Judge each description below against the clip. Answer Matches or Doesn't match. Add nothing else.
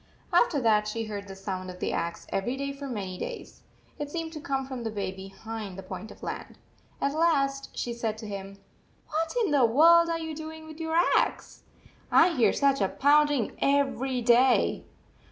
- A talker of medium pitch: Doesn't match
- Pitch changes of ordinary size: Doesn't match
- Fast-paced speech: Doesn't match